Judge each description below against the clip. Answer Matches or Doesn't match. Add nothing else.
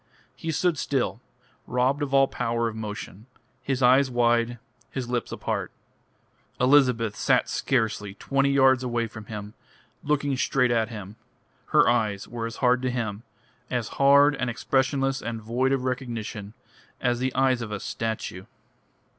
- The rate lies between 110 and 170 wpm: Matches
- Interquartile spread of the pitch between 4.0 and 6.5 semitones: Doesn't match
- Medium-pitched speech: Doesn't match